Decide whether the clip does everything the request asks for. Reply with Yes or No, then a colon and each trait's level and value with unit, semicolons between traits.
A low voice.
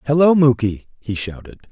Yes: low, 130 Hz